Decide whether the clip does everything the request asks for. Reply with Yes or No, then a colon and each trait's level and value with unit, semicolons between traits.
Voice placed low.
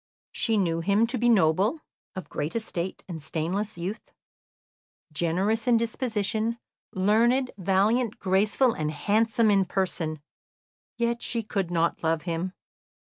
No: high, 200 Hz